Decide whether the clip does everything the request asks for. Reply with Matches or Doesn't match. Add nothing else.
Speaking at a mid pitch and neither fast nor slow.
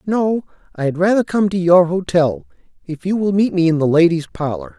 Doesn't match